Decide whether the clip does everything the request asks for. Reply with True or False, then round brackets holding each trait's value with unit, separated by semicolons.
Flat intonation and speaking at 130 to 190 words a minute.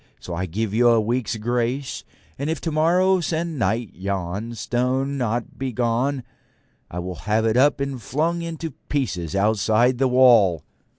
False (4.5 semitones; 155 wpm)